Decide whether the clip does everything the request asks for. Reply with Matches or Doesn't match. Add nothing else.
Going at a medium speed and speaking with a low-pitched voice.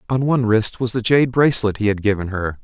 Doesn't match